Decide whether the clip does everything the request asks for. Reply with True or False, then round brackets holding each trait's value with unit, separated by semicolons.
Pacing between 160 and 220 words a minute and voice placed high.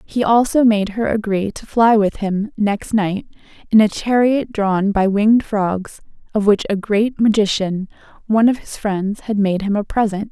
True (185 wpm; 210 Hz)